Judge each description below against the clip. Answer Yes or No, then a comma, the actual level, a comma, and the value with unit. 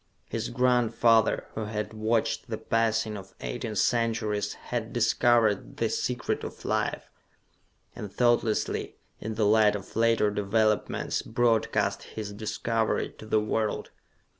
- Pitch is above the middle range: No, low, 110 Hz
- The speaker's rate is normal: No, slow, 125 wpm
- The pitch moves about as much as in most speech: No, narrow, 1.4 semitones